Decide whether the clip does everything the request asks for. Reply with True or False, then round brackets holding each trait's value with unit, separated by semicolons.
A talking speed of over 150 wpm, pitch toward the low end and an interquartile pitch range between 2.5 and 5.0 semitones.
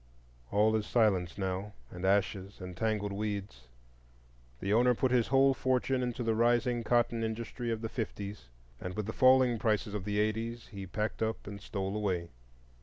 True (175 wpm; 110 Hz; 3.0 semitones)